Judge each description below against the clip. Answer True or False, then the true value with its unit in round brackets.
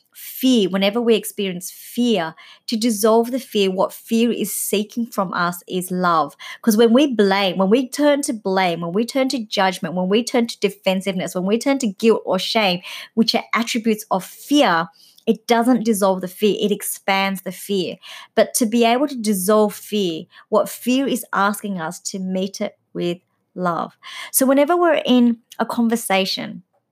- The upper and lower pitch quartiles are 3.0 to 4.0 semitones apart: True (3.7 semitones)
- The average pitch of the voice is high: True (210 Hz)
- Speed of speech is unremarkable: True (180 wpm)